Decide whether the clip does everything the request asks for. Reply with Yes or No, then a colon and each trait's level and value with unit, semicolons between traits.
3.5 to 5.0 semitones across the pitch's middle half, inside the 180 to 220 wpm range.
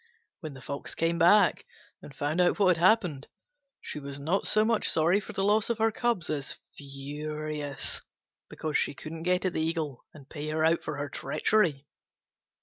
Yes: average, 4.0 semitones; average, 185 wpm